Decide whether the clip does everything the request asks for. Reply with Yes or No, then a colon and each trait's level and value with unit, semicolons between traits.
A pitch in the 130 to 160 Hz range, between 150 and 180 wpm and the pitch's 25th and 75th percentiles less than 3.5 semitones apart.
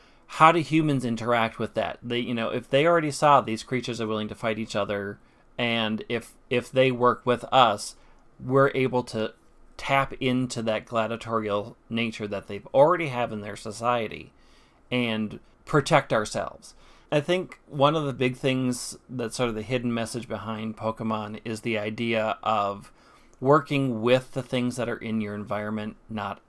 No: low, 115 Hz; average, 170 wpm; average, 2.7 semitones